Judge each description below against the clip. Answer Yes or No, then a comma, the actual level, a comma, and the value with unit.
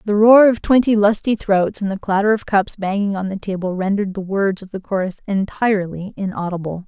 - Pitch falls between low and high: No, high, 200 Hz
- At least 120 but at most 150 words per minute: No, average, 200 wpm